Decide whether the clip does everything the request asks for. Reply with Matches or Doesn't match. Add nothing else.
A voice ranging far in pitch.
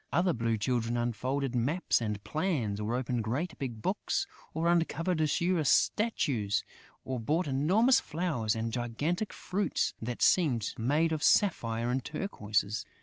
Matches